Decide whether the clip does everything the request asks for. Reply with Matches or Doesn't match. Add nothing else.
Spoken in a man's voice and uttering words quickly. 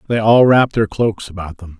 Matches